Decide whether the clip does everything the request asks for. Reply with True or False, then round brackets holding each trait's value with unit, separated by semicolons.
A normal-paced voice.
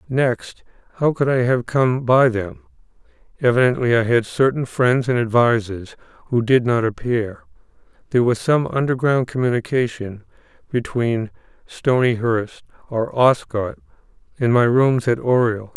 False (125 wpm)